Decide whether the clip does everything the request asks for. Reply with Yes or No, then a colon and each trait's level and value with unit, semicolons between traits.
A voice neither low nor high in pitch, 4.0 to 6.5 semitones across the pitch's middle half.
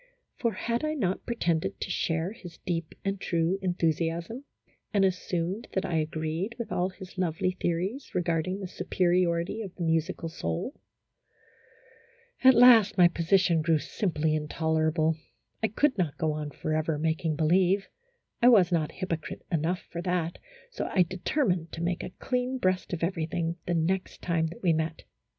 No: medium, 175 Hz; average, 2.9 semitones